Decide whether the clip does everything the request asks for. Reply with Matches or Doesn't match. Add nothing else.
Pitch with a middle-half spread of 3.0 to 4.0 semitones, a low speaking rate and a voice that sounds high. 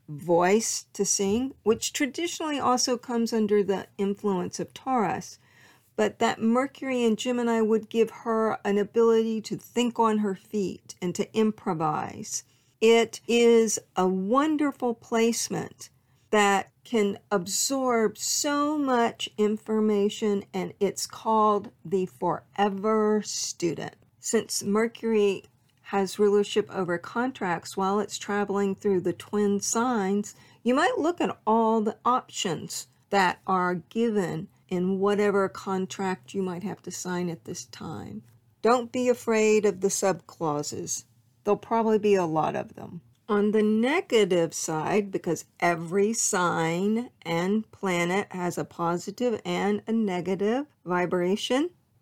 Matches